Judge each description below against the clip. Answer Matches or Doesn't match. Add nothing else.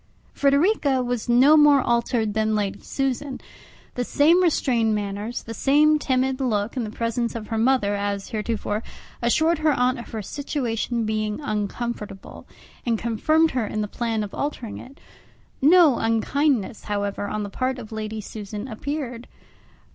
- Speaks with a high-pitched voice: Matches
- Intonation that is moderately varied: Matches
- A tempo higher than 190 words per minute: Doesn't match